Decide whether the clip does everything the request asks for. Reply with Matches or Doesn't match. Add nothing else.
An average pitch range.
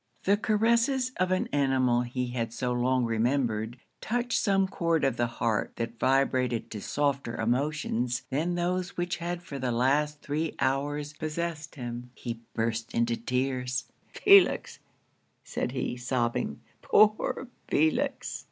Doesn't match